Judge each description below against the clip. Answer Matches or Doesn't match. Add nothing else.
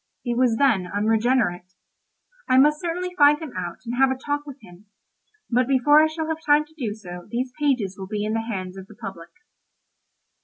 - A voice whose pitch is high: Matches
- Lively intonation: Matches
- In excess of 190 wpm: Matches